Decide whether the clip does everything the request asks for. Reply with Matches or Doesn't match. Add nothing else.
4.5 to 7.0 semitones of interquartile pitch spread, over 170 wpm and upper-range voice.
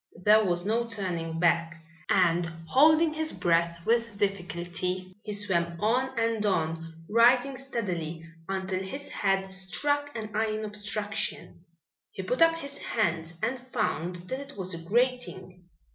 Doesn't match